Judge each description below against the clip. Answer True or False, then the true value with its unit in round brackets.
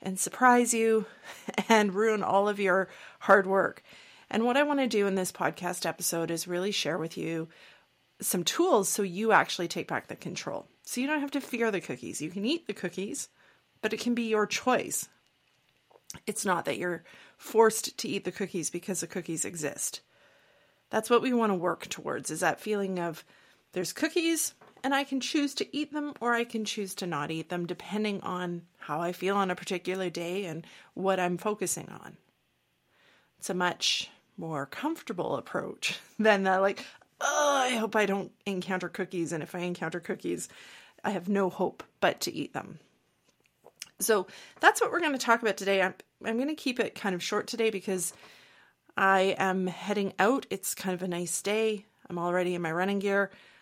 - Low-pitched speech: False (195 Hz)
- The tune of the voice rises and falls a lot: False (3.9 semitones)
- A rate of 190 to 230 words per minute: True (195 wpm)